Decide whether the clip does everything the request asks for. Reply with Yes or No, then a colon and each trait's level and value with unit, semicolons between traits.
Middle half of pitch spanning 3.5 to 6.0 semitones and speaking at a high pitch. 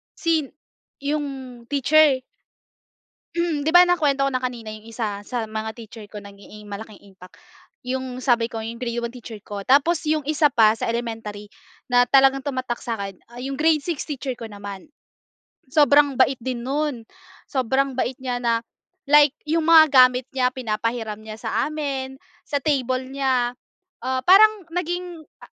Yes: average, 4.0 semitones; very high, 255 Hz